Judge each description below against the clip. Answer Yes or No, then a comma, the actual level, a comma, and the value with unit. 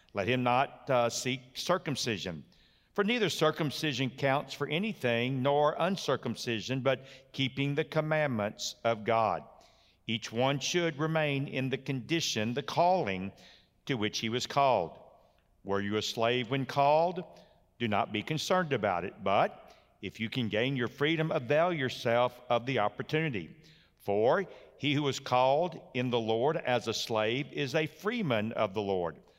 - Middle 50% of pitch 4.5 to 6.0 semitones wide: Yes, average, 4.9 semitones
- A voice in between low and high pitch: No, low, 130 Hz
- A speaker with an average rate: Yes, average, 155 wpm